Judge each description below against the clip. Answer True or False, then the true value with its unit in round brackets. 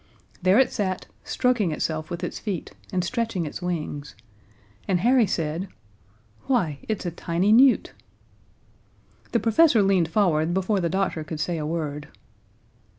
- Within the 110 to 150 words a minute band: True (145 wpm)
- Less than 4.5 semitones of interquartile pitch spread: False (4.8 semitones)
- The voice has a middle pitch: True (180 Hz)